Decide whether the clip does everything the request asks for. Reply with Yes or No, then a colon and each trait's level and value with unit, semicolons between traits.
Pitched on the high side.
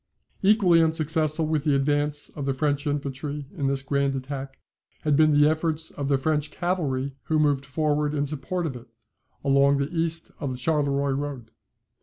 No: medium, 145 Hz